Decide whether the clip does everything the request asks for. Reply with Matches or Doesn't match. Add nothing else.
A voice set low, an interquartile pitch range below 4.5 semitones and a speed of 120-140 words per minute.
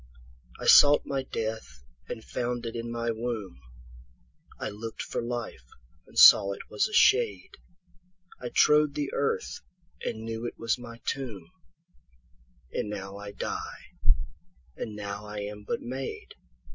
Doesn't match